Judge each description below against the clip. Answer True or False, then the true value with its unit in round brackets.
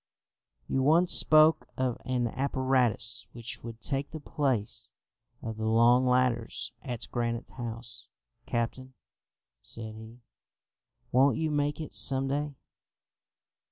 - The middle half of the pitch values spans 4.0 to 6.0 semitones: False (3.0 semitones)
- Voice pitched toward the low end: True (125 Hz)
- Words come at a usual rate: False (120 wpm)